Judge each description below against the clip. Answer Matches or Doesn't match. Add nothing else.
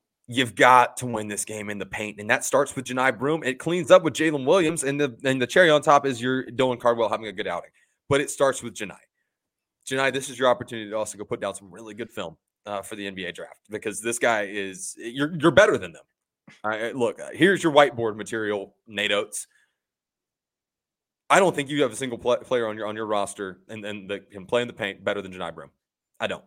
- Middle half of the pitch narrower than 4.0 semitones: Doesn't match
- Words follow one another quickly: Matches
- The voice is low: Matches